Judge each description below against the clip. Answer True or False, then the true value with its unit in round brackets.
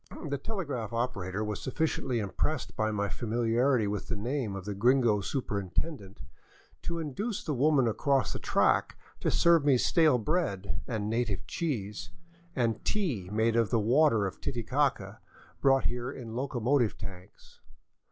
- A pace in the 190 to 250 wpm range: False (145 wpm)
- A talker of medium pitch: False (120 Hz)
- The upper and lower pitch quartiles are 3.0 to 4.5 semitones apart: False (5.1 semitones)